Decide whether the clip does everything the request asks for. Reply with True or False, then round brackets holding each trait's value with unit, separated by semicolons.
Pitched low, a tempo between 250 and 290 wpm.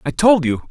False (175 Hz; 255 wpm)